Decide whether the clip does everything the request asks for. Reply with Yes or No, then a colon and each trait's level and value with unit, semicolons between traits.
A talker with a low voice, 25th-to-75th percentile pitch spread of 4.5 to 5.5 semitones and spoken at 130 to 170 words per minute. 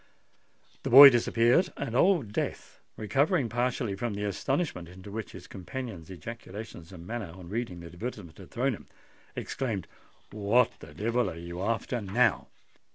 Yes: low, 110 Hz; average, 4.8 semitones; average, 155 wpm